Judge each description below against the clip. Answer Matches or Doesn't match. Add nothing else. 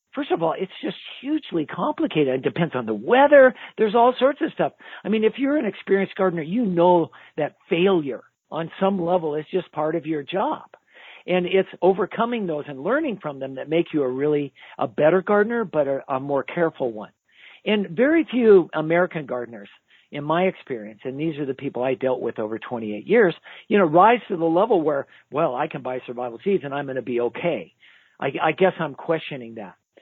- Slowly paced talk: Doesn't match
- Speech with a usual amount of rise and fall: Doesn't match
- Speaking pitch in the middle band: Matches